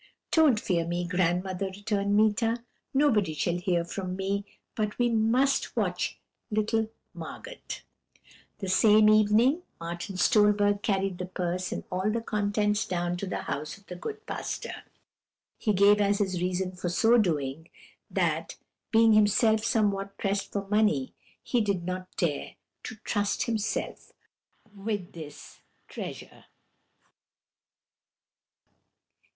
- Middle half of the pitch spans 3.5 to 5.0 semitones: No, average, 3.0 semitones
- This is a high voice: Yes, high, 200 Hz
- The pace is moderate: No, slow, 125 wpm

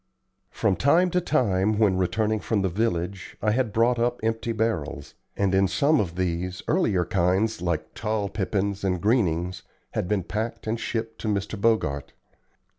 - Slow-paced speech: No, average, 165 wpm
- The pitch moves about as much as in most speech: Yes, average, 3.6 semitones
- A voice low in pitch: Yes, low, 105 Hz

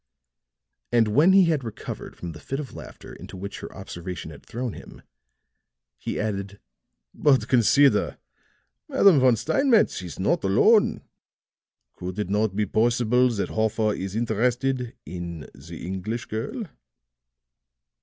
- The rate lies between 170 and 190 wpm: No, slow, 135 wpm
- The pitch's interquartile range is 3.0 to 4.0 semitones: No, average, 4.9 semitones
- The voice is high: No, low, 110 Hz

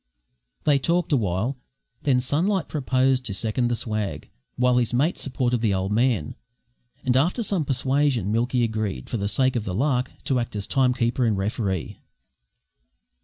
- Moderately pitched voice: No, low, 125 Hz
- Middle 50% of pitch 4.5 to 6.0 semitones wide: No, average, 3.8 semitones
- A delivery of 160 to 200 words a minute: Yes, average, 165 wpm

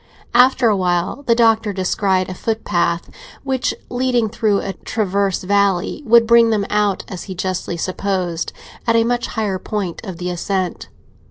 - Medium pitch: No, high, 200 Hz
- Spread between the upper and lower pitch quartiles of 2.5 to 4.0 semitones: Yes, average, 3.6 semitones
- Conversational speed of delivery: Yes, average, 160 wpm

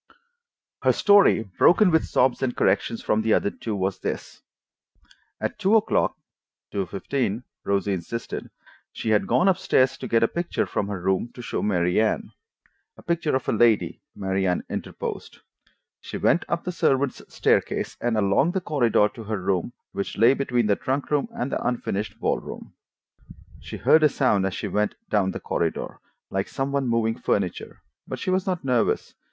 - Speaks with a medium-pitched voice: No, low, 115 Hz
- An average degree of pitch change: No, wide, 5.8 semitones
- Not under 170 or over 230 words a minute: Yes, average, 180 wpm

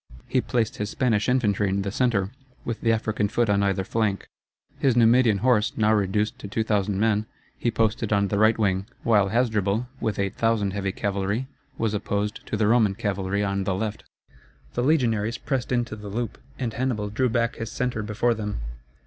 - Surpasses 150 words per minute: Yes, average, 185 wpm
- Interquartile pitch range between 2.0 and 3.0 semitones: Yes, narrow, 2.5 semitones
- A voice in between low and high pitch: No, low, 105 Hz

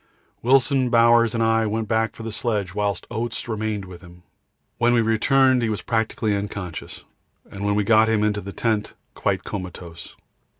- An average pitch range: No, narrow, 2.2 semitones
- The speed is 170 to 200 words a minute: Yes, average, 175 wpm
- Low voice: Yes, low, 110 Hz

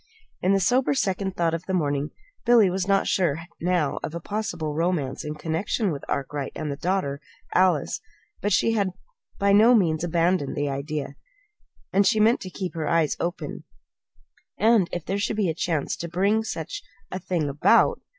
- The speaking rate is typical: Yes, average, 180 wpm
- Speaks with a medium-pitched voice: Yes, medium, 175 Hz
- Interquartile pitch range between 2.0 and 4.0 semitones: No, average, 4.4 semitones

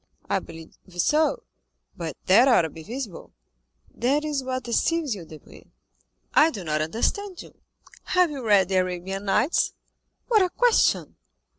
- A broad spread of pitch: Yes, wide, 9.0 semitones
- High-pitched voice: Yes, high, 235 Hz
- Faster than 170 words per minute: No, average, 150 wpm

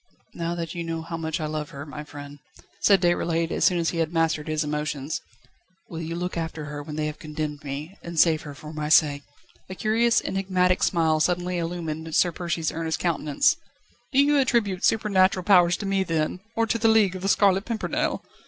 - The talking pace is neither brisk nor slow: No, fast, 210 wpm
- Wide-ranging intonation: No, average, 3.3 semitones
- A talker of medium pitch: Yes, medium, 165 Hz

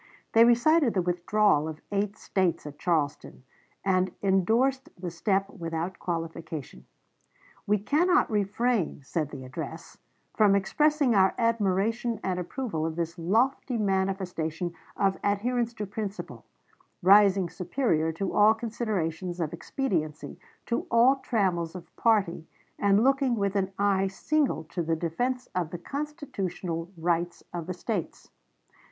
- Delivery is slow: Yes, slow, 130 wpm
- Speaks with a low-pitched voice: No, high, 195 Hz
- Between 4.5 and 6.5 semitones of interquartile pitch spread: Yes, average, 5.2 semitones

